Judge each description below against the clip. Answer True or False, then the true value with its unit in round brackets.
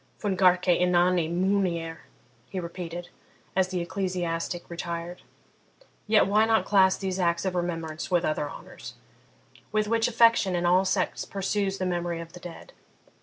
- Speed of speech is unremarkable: True (150 wpm)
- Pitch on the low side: False (180 Hz)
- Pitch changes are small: True (2.0 semitones)